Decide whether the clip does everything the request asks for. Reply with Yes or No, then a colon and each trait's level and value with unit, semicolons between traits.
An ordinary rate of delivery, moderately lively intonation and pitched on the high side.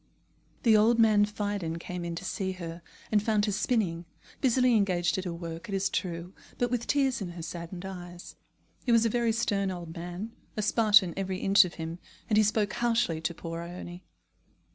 Yes: average, 195 wpm; average, 3.8 semitones; high, 195 Hz